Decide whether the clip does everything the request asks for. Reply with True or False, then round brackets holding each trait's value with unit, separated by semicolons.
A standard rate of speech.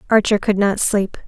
True (190 wpm)